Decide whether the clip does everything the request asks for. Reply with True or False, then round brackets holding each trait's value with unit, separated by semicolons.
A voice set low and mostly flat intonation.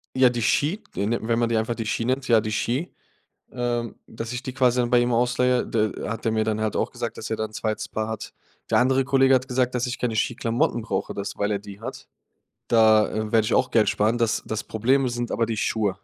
True (115 Hz; 2.2 semitones)